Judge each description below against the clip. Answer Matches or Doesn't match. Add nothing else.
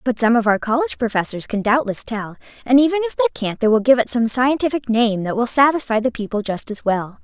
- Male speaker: Doesn't match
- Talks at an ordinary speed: Doesn't match